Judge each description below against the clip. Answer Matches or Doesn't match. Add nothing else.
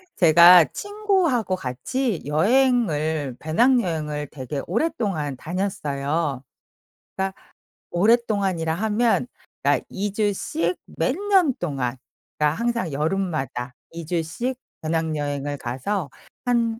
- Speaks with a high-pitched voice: Doesn't match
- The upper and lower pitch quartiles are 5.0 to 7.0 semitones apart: Doesn't match